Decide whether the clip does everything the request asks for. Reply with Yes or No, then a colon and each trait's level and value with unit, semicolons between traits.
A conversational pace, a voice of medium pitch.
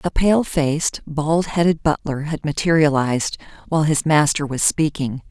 Yes: average, 145 wpm; medium, 155 Hz